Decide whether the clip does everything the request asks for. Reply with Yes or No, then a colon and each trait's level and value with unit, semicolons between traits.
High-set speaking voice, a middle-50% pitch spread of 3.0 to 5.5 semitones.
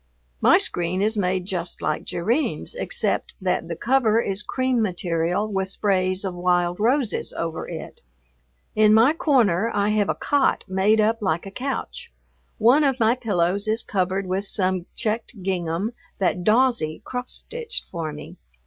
Yes: high, 200 Hz; average, 4.3 semitones